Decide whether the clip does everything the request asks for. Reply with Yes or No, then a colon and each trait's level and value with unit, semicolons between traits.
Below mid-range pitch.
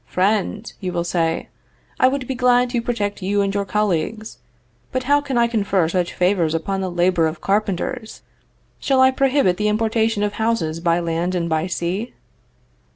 No: high, 200 Hz